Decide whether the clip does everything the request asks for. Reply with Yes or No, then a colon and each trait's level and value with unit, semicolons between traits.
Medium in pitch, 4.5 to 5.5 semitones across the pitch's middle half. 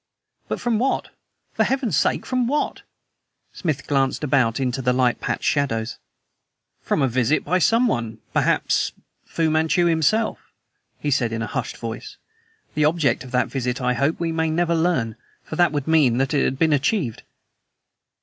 Yes: medium, 145 Hz; average, 5.0 semitones